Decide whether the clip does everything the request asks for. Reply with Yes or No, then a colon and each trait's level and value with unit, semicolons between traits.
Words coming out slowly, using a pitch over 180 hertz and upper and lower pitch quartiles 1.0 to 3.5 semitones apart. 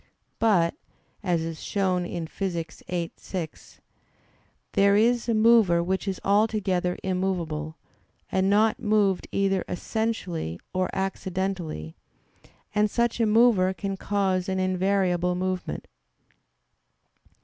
Yes: slow, 110 wpm; high, 190 Hz; narrow, 2.5 semitones